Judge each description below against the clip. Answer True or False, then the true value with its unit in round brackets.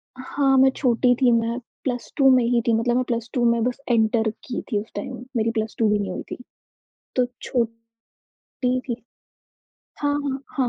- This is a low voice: False (240 Hz)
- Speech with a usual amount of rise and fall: False (1.9 semitones)